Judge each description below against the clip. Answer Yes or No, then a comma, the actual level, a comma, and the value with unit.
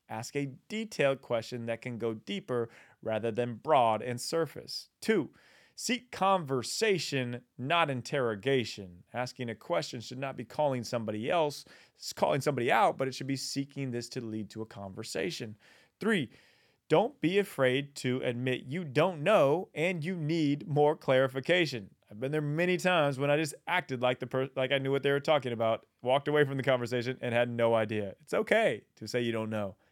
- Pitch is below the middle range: Yes, low, 130 Hz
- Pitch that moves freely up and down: No, average, 3.8 semitones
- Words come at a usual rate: Yes, average, 185 wpm